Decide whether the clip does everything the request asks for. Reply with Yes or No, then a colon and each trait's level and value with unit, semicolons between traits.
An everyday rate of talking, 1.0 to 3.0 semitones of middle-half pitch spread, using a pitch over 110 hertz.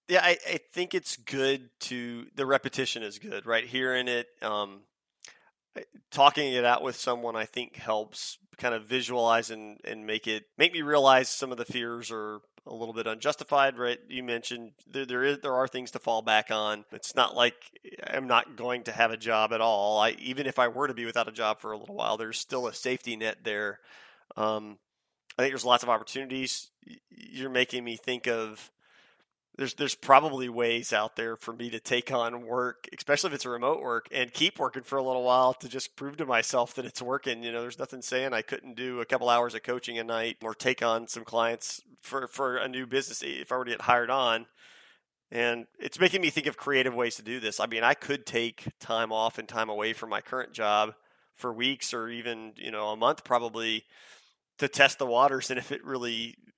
No: fast, 220 wpm; narrow, 2.5 semitones; low, 120 Hz